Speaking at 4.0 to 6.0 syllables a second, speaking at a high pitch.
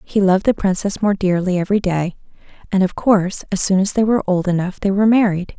No: 6.3 syllables/s; high, 195 Hz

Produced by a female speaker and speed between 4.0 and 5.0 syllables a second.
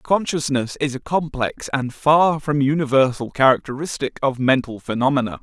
No: male; 4.9 syllables/s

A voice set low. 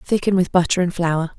No: medium, 175 Hz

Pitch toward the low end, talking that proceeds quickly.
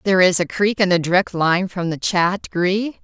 No: medium, 185 Hz; fast, 235 wpm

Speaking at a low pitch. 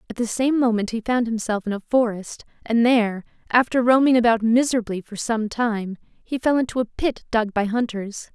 No: high, 230 Hz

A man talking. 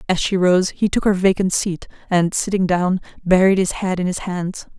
No: female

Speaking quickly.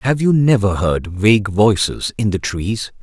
No: average, 180 wpm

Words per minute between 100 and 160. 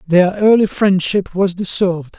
Yes: slow, 135 wpm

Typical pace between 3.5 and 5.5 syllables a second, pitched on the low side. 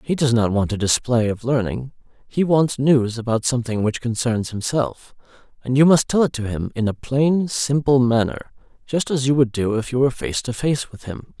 Yes: 5.1 syllables/s; low, 125 Hz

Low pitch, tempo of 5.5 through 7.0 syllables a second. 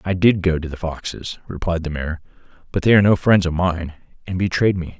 Yes: very low, 90 Hz; 5.7 syllables/s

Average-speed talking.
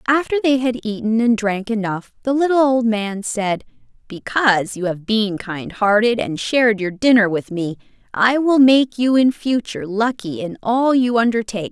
Yes: average, 180 wpm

